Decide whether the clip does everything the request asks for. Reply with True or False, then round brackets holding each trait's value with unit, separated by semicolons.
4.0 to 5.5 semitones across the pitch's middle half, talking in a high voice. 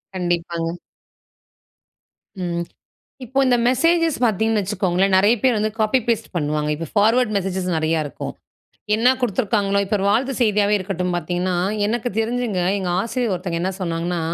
True (4.3 semitones; 200 Hz)